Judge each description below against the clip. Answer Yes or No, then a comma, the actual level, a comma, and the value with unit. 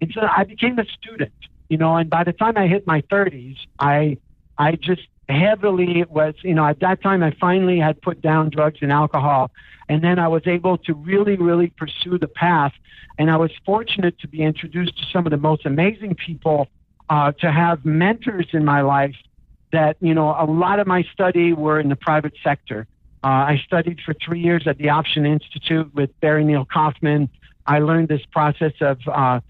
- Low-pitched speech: No, medium, 160 Hz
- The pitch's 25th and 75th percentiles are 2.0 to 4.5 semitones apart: Yes, average, 2.8 semitones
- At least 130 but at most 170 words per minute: No, average, 200 wpm